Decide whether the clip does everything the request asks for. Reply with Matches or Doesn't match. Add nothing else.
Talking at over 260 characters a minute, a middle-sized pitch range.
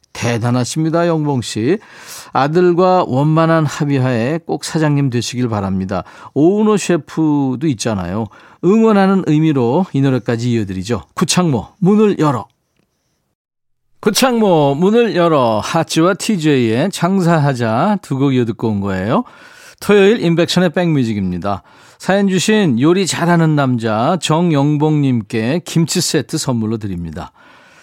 Doesn't match